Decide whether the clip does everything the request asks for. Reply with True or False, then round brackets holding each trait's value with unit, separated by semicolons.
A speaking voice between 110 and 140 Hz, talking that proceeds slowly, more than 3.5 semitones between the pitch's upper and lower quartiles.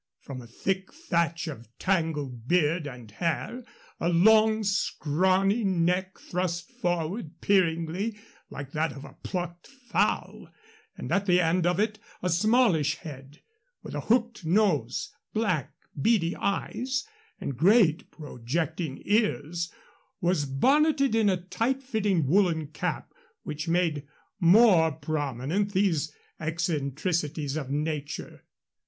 False (170 Hz; 120 wpm; 4.8 semitones)